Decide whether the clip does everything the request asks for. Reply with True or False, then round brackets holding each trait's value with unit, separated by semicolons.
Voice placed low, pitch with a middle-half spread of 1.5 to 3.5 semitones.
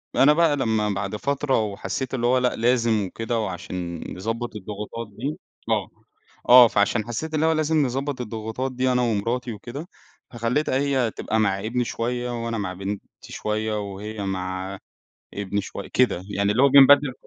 False (115 Hz; 3.9 semitones)